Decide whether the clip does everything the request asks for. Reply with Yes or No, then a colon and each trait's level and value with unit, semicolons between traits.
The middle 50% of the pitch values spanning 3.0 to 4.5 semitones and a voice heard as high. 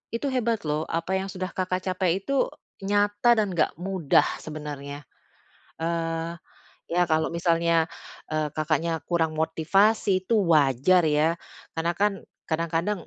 No: average, 3.4 semitones; medium, 170 Hz